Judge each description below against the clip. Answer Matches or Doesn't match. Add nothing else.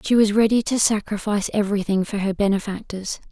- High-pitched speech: Matches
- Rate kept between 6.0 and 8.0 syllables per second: Matches